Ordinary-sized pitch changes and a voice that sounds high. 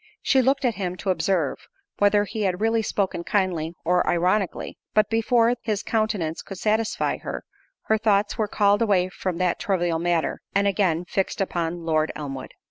Yes: average, 3.6 semitones; high, 195 Hz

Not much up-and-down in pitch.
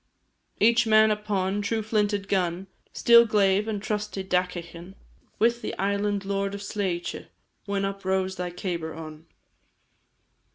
Yes: narrow, 2.2 semitones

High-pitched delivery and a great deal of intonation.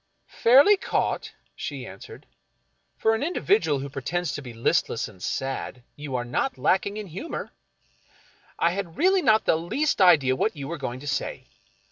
No: medium, 170 Hz; wide, 8.7 semitones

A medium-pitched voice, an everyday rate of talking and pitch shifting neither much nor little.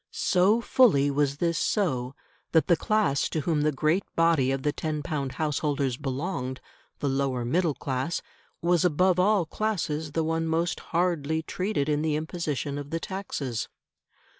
Yes: medium, 155 Hz; average, 160 wpm; average, 3.8 semitones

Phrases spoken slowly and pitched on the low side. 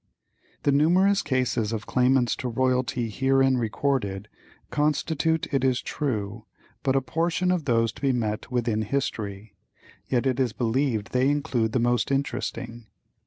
No: average, 150 wpm; low, 130 Hz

